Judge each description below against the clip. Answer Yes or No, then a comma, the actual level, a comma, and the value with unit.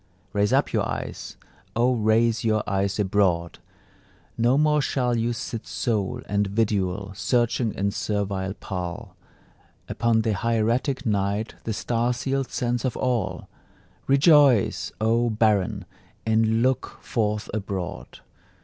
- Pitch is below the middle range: Yes, low, 110 Hz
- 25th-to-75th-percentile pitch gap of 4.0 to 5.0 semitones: No, average, 3.0 semitones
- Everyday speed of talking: No, slow, 120 wpm